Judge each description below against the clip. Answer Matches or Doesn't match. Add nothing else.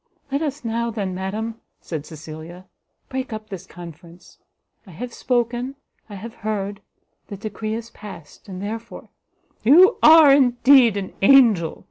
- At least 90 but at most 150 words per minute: Matches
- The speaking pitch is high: Matches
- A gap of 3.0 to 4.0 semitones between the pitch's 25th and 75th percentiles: Doesn't match